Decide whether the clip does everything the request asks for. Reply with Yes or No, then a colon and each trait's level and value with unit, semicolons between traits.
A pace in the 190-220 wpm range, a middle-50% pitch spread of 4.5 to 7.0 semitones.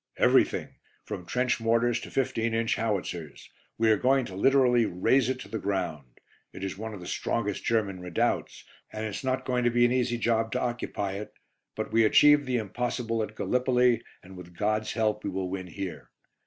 No: average, 195 wpm; average, 3.8 semitones